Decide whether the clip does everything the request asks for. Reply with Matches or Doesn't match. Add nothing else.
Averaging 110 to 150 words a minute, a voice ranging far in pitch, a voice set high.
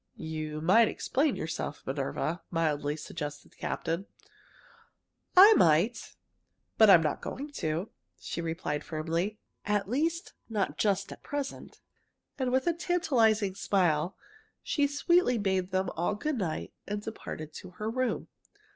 Matches